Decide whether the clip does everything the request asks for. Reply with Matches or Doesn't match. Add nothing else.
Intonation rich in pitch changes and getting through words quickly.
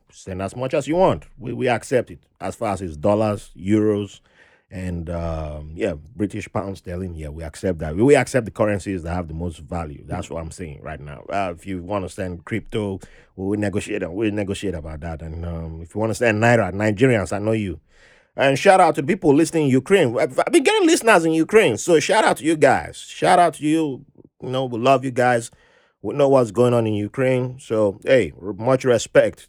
Matches